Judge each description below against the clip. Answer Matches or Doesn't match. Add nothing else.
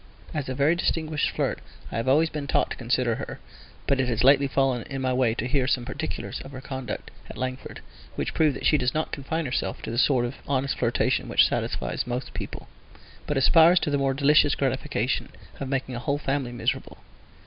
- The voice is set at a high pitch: Doesn't match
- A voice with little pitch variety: Matches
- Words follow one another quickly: Matches